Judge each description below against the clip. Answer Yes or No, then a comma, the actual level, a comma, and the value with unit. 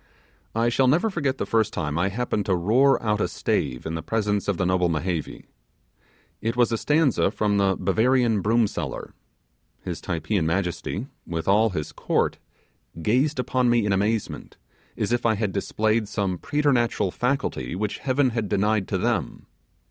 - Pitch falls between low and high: No, low, 105 Hz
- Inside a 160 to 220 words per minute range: Yes, average, 165 wpm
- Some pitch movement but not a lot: Yes, average, 4.3 semitones